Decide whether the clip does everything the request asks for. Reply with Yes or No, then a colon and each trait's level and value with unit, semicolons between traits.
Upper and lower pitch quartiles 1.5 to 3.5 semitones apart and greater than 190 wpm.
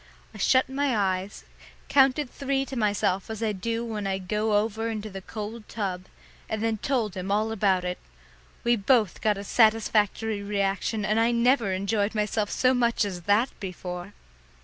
No: narrow, 2.6 semitones; average, 170 wpm